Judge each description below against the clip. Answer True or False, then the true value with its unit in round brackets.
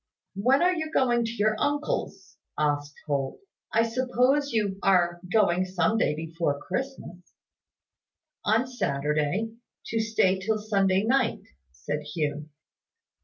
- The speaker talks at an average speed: False (120 wpm)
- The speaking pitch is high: True (200 Hz)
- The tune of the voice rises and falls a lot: True (6.6 semitones)